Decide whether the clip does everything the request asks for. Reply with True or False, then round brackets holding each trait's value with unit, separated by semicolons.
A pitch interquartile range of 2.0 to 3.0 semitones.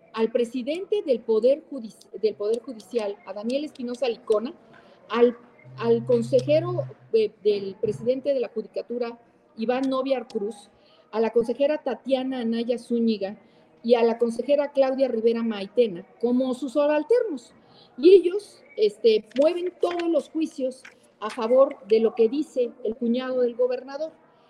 False (3.8 semitones)